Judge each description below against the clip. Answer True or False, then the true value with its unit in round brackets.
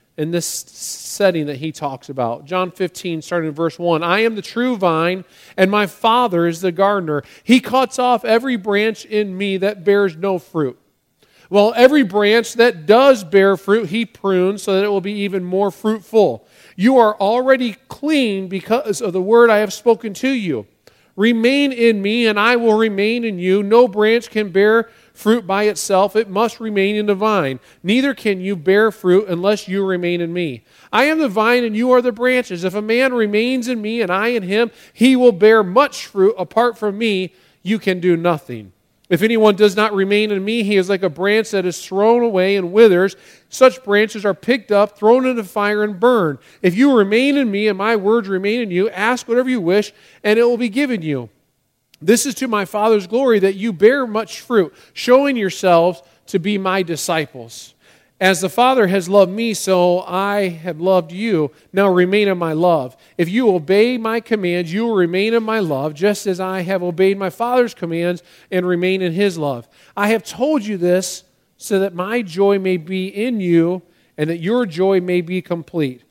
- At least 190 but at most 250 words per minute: True (200 wpm)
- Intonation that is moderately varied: True (3.8 semitones)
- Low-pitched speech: False (205 Hz)